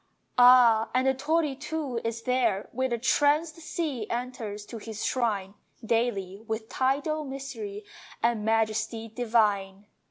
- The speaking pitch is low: No, high, 235 Hz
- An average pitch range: Yes, average, 3.7 semitones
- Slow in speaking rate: Yes, slow, 130 wpm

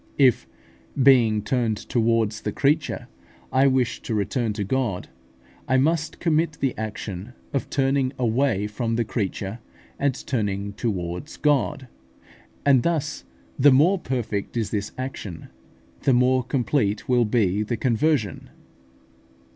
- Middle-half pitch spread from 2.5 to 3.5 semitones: No, average, 4.3 semitones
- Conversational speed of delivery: No, slow, 130 wpm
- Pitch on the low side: Yes, low, 120 Hz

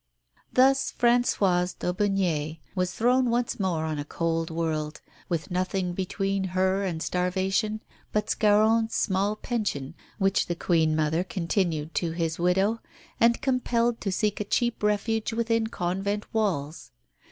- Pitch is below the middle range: No, high, 190 Hz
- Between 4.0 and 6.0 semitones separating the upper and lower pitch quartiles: Yes, average, 4.4 semitones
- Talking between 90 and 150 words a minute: Yes, slow, 135 wpm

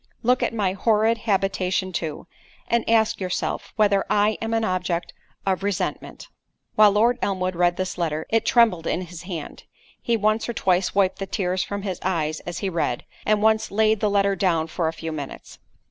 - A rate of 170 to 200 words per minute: Yes, average, 180 wpm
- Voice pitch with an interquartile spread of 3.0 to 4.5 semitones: Yes, average, 3.3 semitones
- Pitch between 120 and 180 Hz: No, high, 195 Hz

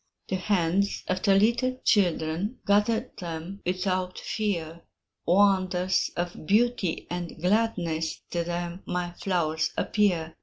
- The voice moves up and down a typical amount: Yes, average, 3.0 semitones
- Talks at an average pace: No, slow, 115 wpm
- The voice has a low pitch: No, medium, 185 Hz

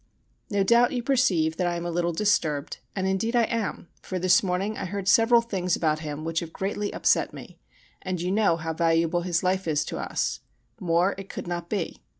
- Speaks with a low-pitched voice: No, medium, 180 Hz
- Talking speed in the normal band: No, fast, 210 wpm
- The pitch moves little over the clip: No, average, 3.3 semitones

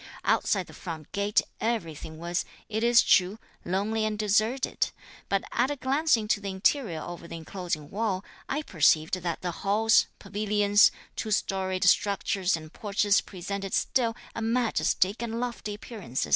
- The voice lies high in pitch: Yes, high, 200 Hz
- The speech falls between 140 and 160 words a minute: Yes, average, 150 wpm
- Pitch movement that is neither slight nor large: Yes, average, 3.6 semitones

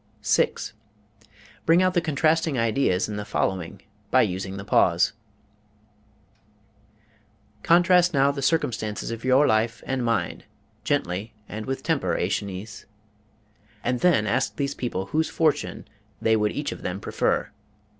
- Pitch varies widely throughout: Yes, wide, 6.7 semitones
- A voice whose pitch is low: Yes, low, 115 Hz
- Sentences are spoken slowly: Yes, slow, 130 wpm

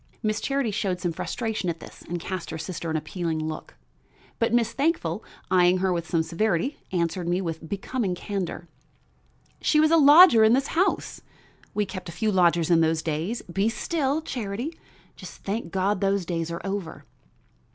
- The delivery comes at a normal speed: Yes, average, 175 wpm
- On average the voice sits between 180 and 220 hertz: Yes, high, 190 Hz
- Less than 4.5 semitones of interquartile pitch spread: No, average, 5.1 semitones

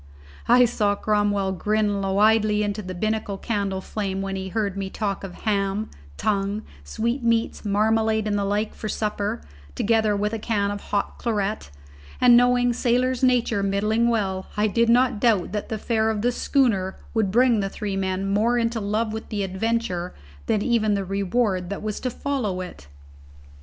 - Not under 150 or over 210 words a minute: Yes, average, 175 wpm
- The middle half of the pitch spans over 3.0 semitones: No, narrow, 2.5 semitones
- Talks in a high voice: Yes, high, 210 Hz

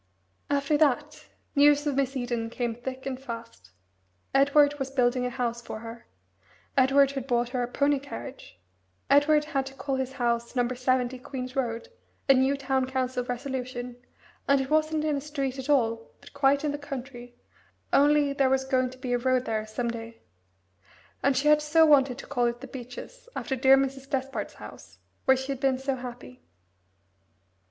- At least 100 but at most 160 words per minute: No, average, 180 wpm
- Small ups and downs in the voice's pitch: Yes, narrow, 2.3 semitones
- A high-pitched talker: Yes, very high, 265 Hz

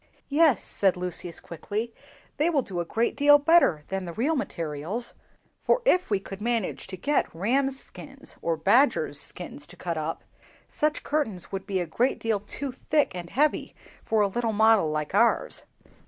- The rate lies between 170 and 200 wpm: Yes, average, 175 wpm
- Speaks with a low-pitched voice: No, high, 210 Hz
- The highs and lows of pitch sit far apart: Yes, wide, 7.4 semitones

